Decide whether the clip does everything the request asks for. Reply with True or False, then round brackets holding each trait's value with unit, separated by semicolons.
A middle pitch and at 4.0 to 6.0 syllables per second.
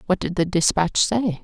True (180 Hz; 4.7 syllables/s)